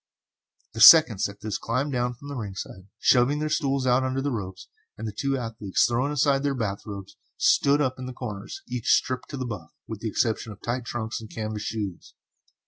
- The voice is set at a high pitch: No, low, 120 Hz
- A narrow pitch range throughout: No, average, 3.9 semitones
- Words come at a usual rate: No, fast, 210 wpm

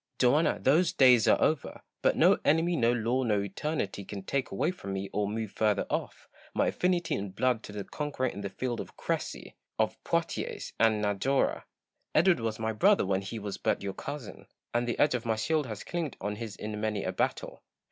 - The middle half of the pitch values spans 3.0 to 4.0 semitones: No, average, 5.2 semitones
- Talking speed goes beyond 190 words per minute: Yes, fast, 205 wpm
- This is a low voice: Yes, low, 115 Hz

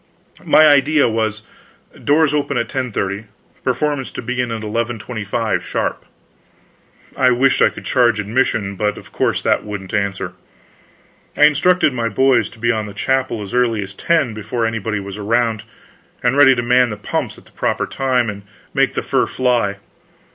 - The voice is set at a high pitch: No, low, 120 Hz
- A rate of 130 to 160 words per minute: No, average, 170 wpm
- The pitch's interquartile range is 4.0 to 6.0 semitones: No, average, 3.6 semitones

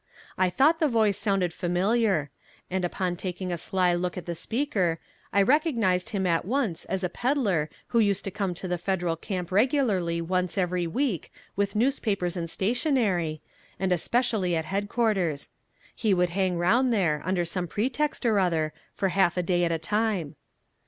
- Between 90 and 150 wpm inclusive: No, average, 170 wpm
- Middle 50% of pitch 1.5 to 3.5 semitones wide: No, average, 3.9 semitones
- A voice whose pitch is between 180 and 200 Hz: Yes, high, 190 Hz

